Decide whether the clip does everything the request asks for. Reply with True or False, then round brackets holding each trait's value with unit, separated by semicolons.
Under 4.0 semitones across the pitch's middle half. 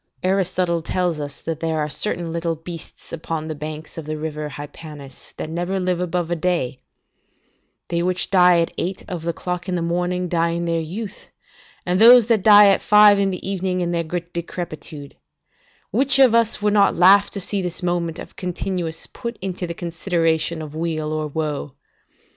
True (2.5 semitones)